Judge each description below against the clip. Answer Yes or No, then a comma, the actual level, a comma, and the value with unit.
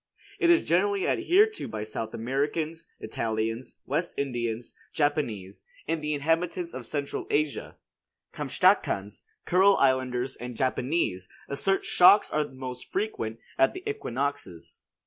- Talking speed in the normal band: No, slow, 125 wpm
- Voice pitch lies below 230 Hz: Yes, medium, 140 Hz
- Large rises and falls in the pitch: Yes, wide, 6.5 semitones